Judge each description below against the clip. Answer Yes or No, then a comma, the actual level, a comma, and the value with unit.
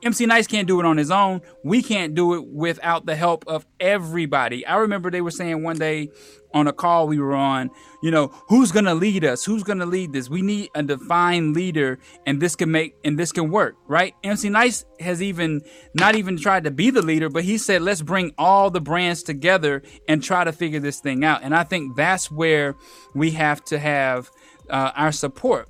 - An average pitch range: Yes, average, 3.9 semitones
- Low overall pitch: No, medium, 165 Hz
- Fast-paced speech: Yes, fast, 220 wpm